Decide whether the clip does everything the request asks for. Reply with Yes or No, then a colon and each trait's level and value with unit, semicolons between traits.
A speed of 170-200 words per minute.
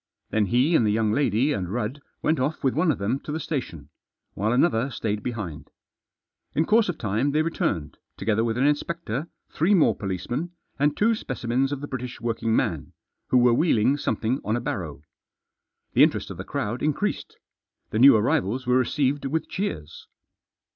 Yes: average, 180 wpm